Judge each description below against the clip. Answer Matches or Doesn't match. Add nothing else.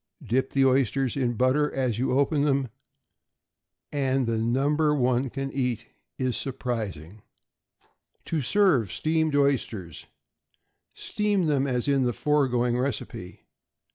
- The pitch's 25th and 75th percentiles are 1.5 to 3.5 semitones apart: Matches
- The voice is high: Doesn't match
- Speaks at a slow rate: Matches